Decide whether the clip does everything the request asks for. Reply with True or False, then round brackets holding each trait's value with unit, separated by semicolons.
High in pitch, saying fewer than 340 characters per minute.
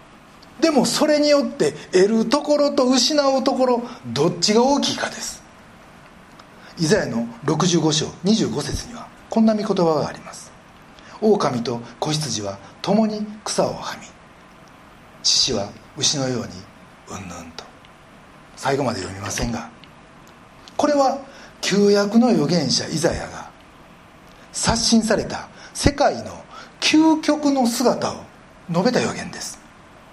True (215 Hz; 230 characters per minute)